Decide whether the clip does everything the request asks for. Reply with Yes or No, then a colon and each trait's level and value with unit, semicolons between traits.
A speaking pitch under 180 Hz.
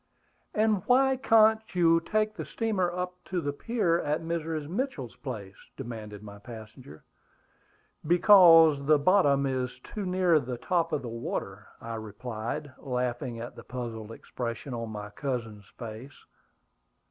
Yes: medium, 140 Hz